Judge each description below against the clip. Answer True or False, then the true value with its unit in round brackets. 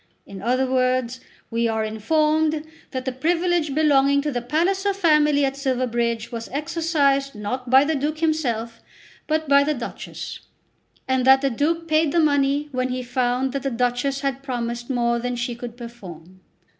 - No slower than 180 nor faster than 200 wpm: False (170 wpm)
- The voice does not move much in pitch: False (3.8 semitones)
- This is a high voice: True (265 Hz)